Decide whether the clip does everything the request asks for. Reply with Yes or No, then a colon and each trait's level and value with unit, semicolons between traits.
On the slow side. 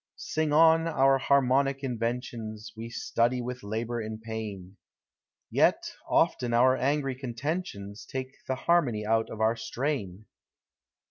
Yes: slow, 125 wpm